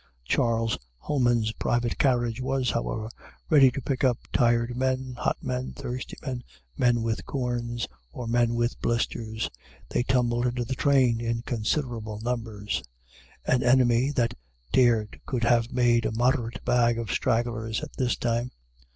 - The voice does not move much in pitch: Yes, narrow, 1.5 semitones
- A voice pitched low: Yes, low, 120 Hz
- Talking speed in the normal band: Yes, average, 145 wpm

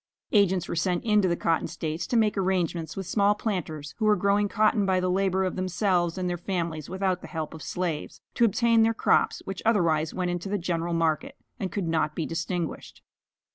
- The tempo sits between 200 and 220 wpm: Yes, fast, 205 wpm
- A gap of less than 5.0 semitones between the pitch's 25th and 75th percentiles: Yes, average, 3.2 semitones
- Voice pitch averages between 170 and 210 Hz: Yes, medium, 185 Hz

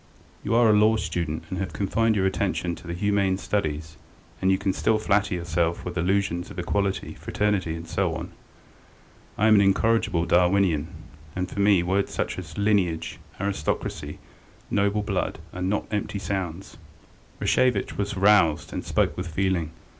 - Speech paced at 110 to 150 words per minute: No, average, 160 wpm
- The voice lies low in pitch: Yes, very low, 95 Hz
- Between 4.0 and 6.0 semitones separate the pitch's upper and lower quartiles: No, average, 2.8 semitones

